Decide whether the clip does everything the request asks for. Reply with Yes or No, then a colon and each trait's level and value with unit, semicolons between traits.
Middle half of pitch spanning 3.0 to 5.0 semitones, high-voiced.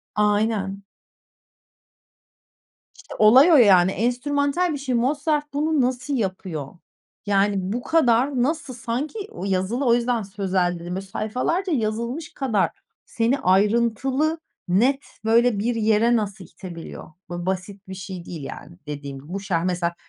No: wide, 5.4 semitones; high, 220 Hz